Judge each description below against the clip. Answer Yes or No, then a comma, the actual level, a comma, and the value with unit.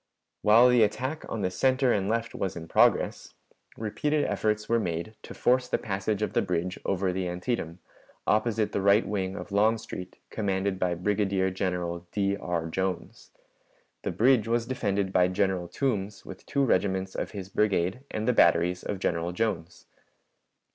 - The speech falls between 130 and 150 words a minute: No, average, 165 wpm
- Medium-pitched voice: No, low, 100 Hz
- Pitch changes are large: No, average, 3.4 semitones